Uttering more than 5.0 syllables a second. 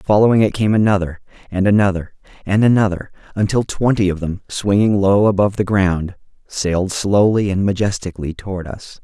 Yes: 5.5 syllables/s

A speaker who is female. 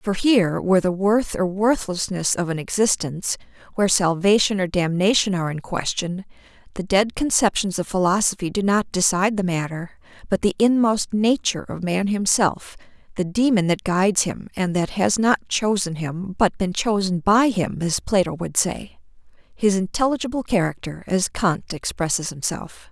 Yes: female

